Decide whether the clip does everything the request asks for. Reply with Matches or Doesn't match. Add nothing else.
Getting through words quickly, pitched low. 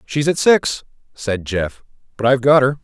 Doesn't match